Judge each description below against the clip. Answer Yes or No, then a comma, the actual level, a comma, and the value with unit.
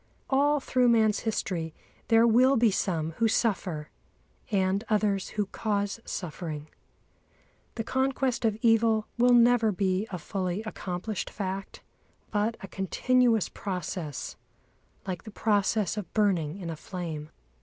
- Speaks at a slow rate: Yes, slow, 130 wpm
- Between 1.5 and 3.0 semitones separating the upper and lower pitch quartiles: No, average, 3.8 semitones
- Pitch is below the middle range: No, high, 205 Hz